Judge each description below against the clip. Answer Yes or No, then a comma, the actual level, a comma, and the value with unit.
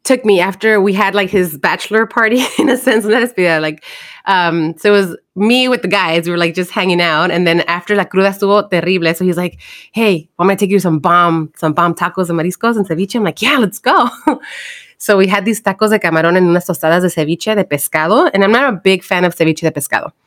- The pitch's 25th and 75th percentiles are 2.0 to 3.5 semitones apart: No, average, 4.0 semitones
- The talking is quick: Yes, fast, 245 wpm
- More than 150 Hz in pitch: Yes, high, 190 Hz